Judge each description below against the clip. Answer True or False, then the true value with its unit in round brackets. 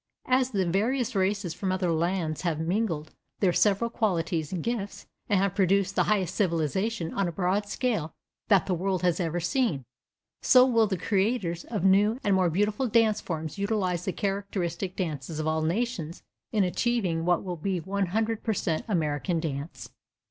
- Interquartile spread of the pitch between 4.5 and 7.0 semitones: False (3.8 semitones)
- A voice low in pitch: False (190 Hz)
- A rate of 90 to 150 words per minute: False (175 wpm)